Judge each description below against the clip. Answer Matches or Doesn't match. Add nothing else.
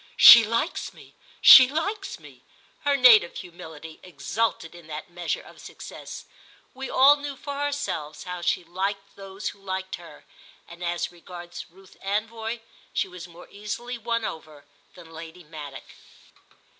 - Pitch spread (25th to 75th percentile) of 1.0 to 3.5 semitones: Doesn't match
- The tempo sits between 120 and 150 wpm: Matches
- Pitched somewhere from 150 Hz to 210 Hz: Matches